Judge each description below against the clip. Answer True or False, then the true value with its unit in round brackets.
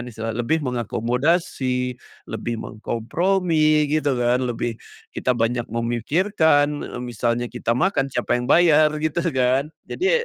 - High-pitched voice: False (130 Hz)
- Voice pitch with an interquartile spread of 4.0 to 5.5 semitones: True (4.6 semitones)